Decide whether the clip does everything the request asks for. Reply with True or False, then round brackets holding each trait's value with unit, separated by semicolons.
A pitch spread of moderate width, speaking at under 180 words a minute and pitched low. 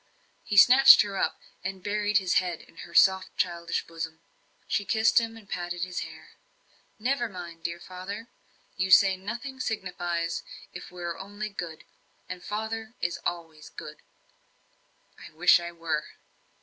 False (3.5 semitones; 150 wpm; 185 Hz)